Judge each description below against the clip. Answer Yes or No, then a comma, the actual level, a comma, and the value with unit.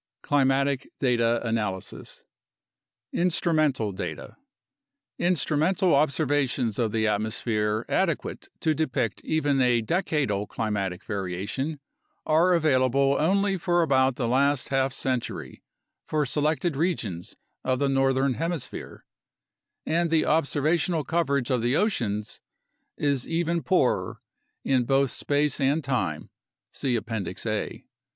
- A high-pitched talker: No, low, 135 Hz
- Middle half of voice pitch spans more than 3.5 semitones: Yes, average, 5.0 semitones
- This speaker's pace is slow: Yes, slow, 115 wpm